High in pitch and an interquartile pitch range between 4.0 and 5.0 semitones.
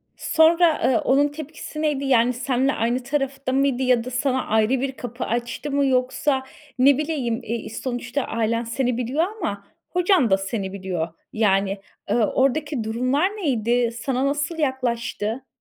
No: very high, 255 Hz; average, 3.4 semitones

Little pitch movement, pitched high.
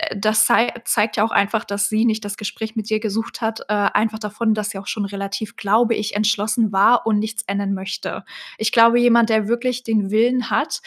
Yes: narrow, 1.8 semitones; high, 215 Hz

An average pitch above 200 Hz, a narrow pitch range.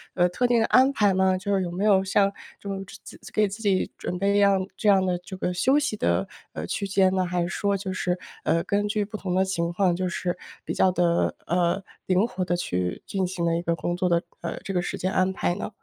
No: high, 190 Hz; narrow, 2.2 semitones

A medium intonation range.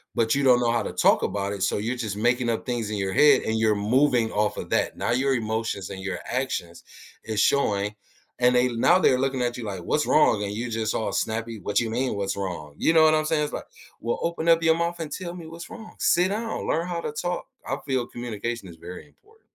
No: wide, 6.0 semitones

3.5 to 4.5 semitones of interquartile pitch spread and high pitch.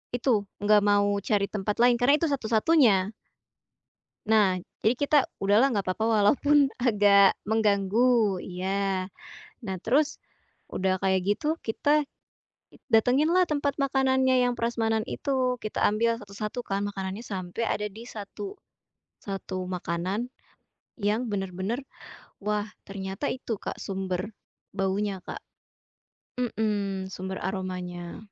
Yes: average, 4.2 semitones; high, 210 Hz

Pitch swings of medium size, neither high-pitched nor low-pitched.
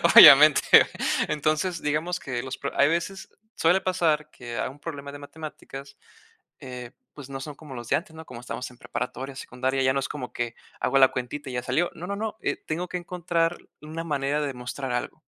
Yes: average, 4.0 semitones; medium, 145 Hz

